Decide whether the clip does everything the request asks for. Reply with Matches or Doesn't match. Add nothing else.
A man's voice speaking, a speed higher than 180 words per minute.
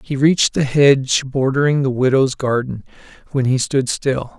Doesn't match